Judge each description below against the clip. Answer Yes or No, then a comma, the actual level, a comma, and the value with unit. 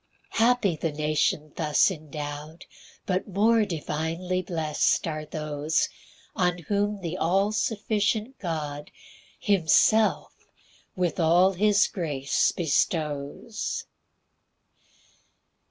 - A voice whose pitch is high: No, medium, 170 Hz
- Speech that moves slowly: Yes, slow, 90 wpm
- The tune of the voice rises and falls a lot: No, average, 4.7 semitones